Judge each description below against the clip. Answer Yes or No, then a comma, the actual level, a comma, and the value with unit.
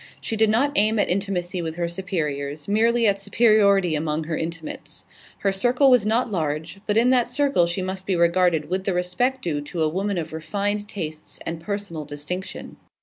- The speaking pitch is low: No, medium, 185 Hz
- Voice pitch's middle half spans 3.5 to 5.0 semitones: Yes, average, 4.4 semitones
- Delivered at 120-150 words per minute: No, average, 190 wpm